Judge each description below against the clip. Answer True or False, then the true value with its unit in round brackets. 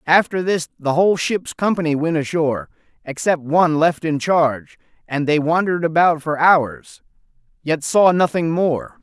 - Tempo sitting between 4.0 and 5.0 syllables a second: True (4.7 syllables/s)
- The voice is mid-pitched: True (160 Hz)